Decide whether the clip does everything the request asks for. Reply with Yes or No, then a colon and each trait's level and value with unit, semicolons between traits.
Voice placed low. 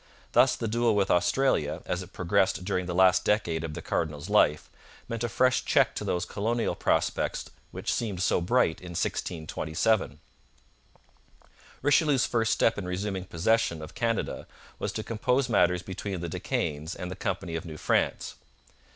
Yes: very low, 95 Hz